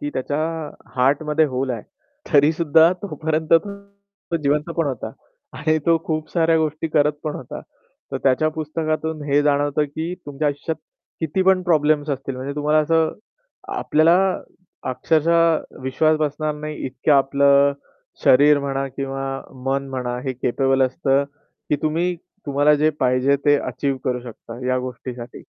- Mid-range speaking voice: Yes, medium, 145 Hz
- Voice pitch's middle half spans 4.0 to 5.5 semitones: No, average, 2.7 semitones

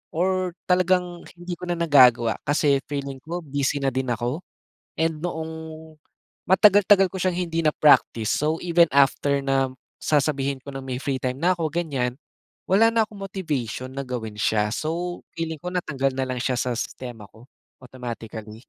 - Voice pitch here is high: No, medium, 145 Hz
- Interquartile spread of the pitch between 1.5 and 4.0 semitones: No, average, 5.2 semitones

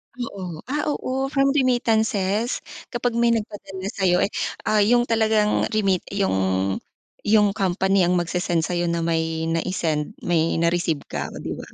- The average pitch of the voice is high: Yes, high, 195 Hz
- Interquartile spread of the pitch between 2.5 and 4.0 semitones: No, average, 4.5 semitones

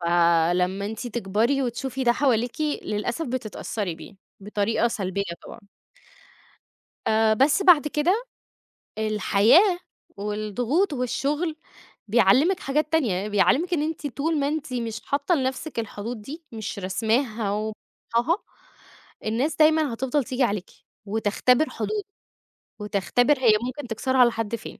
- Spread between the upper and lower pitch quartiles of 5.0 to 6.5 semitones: Yes, wide, 5.6 semitones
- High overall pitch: Yes, high, 240 Hz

